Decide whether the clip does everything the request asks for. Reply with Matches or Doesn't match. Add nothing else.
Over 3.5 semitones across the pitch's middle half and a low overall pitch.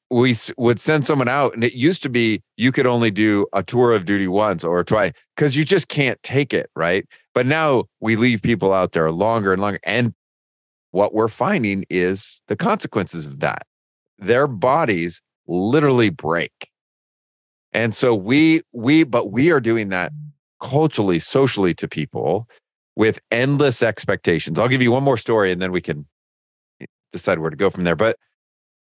Matches